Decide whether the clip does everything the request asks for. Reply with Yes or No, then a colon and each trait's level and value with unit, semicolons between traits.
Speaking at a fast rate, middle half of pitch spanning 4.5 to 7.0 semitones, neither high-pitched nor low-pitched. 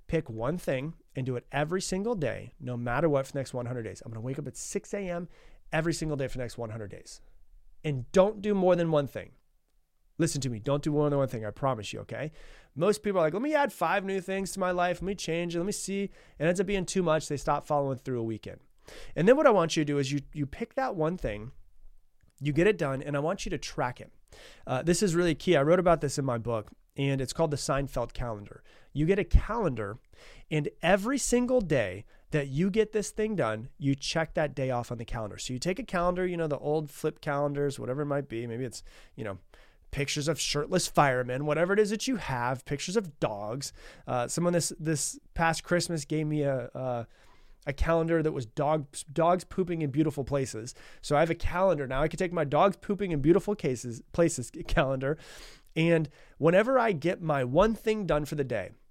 Yes: fast, 235 wpm; average, 5.1 semitones; medium, 150 Hz